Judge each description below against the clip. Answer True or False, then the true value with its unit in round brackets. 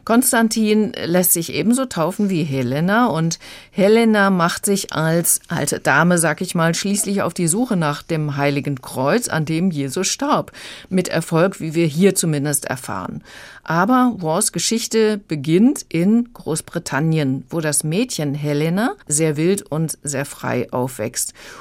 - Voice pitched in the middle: True (170 Hz)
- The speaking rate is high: False (145 wpm)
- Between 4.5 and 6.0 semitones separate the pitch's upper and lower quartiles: True (4.9 semitones)